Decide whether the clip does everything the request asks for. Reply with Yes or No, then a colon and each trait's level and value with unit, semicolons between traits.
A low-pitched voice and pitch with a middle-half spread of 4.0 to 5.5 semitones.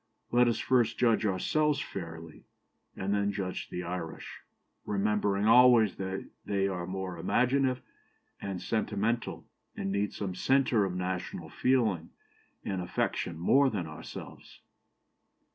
Yes: low, 100 Hz; average, 4.3 semitones